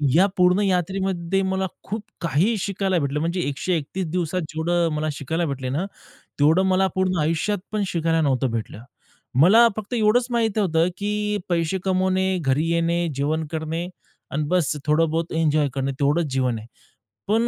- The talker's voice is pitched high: No, medium, 170 Hz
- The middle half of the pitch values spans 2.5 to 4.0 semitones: Yes, average, 3.7 semitones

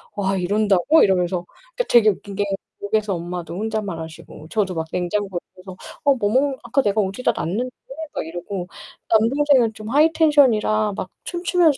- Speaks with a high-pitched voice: Yes, high, 210 Hz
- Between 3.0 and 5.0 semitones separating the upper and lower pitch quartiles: No, wide, 5.4 semitones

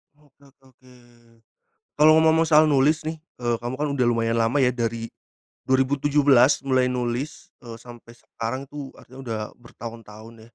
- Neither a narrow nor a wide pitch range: Yes, average, 3.8 semitones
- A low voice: Yes, low, 130 Hz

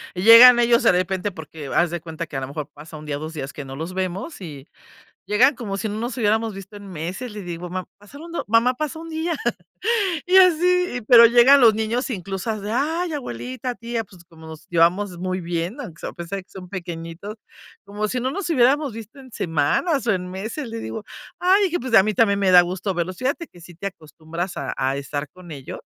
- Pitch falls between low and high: No, high, 200 Hz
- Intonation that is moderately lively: No, wide, 6.2 semitones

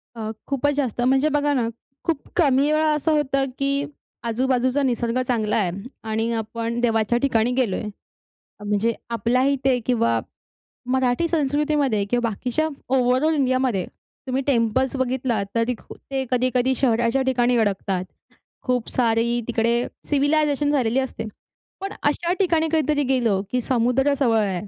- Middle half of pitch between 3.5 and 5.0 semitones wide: No, average, 3.1 semitones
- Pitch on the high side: Yes, very high, 255 Hz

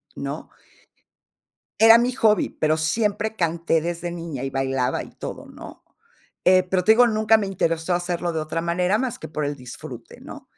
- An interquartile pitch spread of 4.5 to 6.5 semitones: Yes, average, 5.0 semitones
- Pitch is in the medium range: Yes, medium, 175 Hz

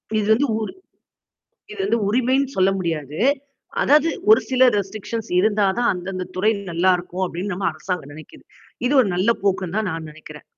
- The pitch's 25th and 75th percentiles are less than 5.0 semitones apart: Yes, average, 4.0 semitones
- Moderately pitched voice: No, high, 195 Hz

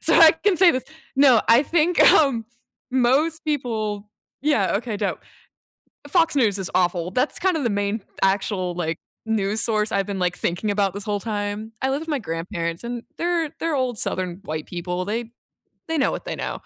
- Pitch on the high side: Yes, high, 220 Hz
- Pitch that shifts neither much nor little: No, wide, 6.3 semitones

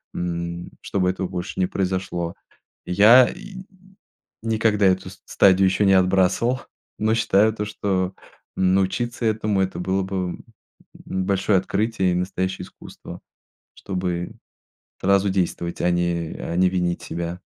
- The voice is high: No, very low, 95 Hz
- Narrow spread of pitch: Yes, narrow, 2.2 semitones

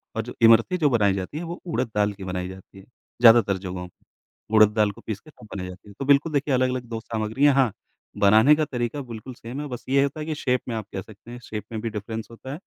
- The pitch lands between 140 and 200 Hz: No, low, 115 Hz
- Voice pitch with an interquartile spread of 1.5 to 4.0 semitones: No, average, 4.7 semitones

